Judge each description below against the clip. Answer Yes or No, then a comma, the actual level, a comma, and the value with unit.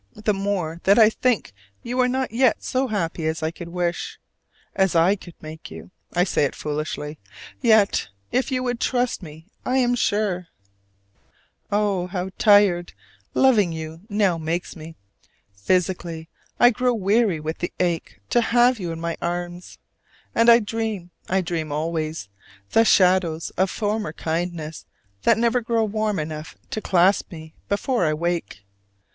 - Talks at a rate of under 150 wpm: No, average, 155 wpm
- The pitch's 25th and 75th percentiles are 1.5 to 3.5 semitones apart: No, average, 5.1 semitones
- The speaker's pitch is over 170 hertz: Yes, medium, 185 Hz